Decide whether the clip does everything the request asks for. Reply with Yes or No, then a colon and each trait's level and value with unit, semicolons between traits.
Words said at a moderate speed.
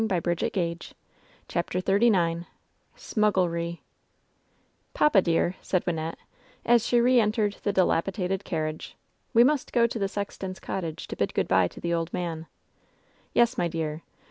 Yes: average, 155 wpm